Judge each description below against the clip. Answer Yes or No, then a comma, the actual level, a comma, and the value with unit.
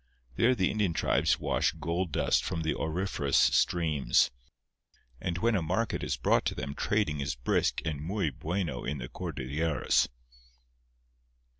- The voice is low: Yes, very low, 80 Hz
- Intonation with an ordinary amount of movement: Yes, average, 4.6 semitones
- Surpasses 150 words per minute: No, average, 145 wpm